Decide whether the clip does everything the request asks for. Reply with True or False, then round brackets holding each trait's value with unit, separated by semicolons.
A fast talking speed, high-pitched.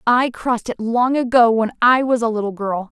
True (220 wpm; 235 Hz)